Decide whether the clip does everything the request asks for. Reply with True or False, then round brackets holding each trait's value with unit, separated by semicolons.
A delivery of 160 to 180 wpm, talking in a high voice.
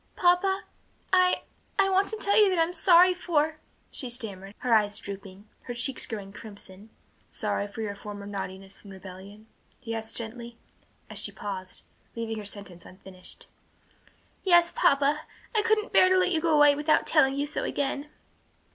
True (170 wpm; 240 Hz)